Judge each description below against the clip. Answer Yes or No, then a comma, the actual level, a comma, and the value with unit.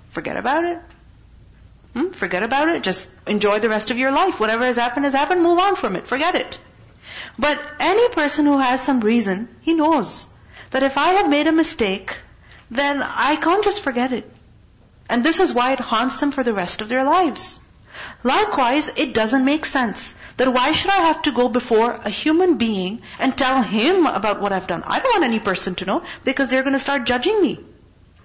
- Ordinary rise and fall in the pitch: No, wide, 5.7 semitones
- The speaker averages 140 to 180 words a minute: No, fast, 205 wpm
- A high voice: Yes, very high, 265 Hz